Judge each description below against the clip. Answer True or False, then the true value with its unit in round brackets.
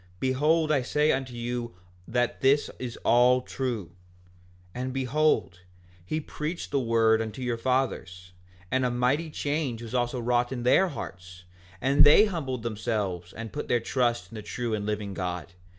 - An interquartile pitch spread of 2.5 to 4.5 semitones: True (3.2 semitones)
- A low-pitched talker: True (120 Hz)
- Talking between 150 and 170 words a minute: True (165 wpm)